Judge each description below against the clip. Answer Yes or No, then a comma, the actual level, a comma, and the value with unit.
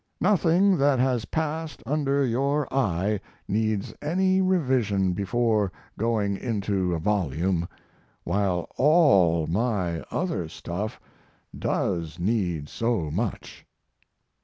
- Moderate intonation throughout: No, wide, 7.2 semitones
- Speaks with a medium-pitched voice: No, low, 110 Hz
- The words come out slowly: Yes, slow, 100 wpm